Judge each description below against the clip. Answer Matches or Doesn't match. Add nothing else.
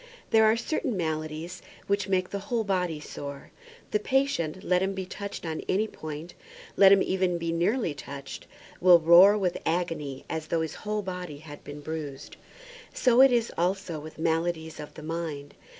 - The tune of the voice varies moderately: Matches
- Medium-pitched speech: Matches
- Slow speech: Doesn't match